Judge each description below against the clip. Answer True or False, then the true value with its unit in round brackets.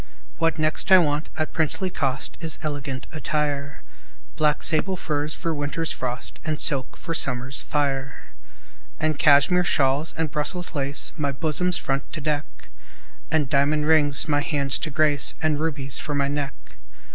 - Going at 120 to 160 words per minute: True (155 wpm)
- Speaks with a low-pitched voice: False (150 Hz)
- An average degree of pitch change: False (2.0 semitones)